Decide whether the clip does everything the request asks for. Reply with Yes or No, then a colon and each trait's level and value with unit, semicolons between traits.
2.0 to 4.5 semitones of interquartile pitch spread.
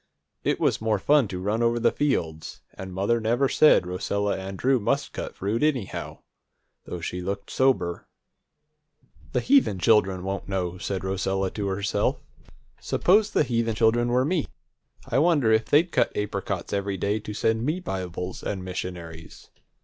Yes: average, 4.2 semitones